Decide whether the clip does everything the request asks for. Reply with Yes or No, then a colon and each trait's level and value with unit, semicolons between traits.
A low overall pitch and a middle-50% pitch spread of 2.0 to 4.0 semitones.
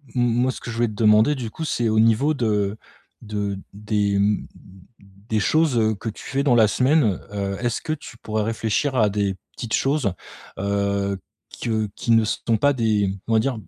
Yes: low, 110 Hz; average, 2.8 semitones